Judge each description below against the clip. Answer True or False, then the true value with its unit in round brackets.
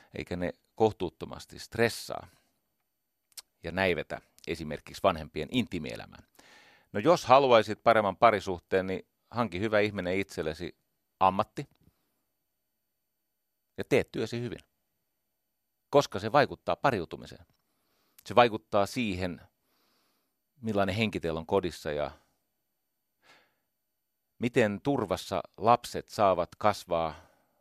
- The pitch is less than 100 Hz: False (105 Hz)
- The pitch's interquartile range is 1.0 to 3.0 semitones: False (3.6 semitones)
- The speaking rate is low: True (90 wpm)